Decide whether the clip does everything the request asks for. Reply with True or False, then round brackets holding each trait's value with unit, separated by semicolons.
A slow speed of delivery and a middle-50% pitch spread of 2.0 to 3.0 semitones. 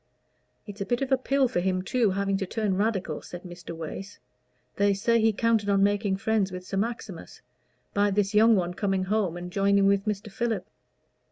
False (195 wpm; 2.5 semitones)